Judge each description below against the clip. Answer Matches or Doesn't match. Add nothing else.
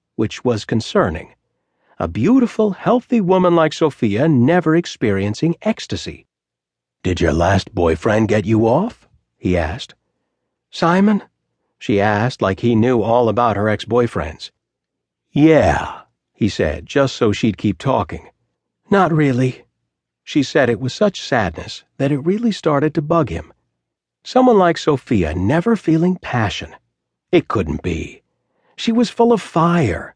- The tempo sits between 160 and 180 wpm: Doesn't match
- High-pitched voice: Doesn't match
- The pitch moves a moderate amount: Doesn't match